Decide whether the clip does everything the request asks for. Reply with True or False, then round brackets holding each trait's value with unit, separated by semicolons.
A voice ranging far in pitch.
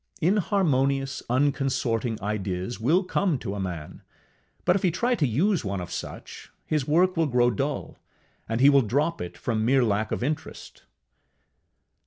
True (6.2 semitones)